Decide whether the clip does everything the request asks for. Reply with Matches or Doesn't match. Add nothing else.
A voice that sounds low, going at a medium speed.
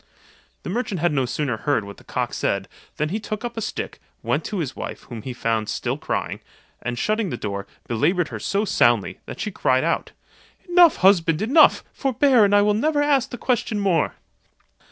Doesn't match